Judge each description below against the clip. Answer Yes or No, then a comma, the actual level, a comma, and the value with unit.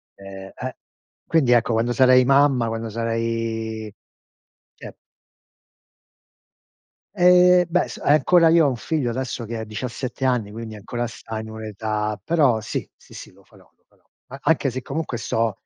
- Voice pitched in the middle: No, low, 120 Hz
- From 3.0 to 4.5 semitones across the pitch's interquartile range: Yes, average, 3.5 semitones